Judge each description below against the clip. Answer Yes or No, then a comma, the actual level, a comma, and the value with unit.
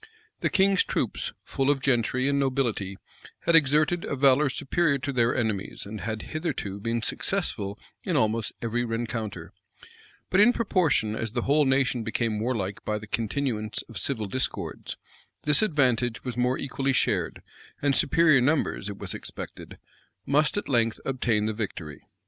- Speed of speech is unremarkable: Yes, average, 155 wpm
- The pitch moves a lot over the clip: No, average, 4.3 semitones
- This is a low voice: Yes, low, 125 Hz